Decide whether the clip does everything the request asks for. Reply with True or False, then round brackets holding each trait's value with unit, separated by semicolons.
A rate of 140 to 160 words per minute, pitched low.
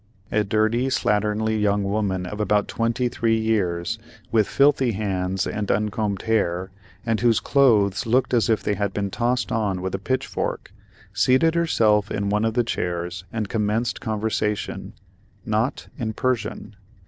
True (150 wpm; 110 Hz)